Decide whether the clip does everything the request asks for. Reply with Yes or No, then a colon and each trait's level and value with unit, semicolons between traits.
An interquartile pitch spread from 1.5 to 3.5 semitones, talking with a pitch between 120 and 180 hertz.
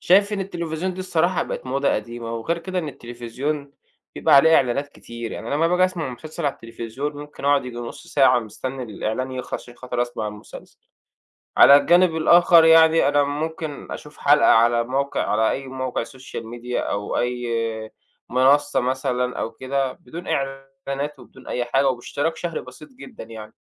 No: average, 4.7 semitones; low, 135 Hz